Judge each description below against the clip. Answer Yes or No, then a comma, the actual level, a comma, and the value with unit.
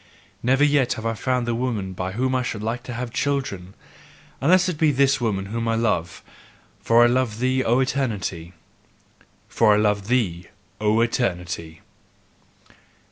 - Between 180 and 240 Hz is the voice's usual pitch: No, low, 115 Hz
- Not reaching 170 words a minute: Yes, average, 160 wpm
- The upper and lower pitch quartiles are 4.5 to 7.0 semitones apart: No, average, 4.1 semitones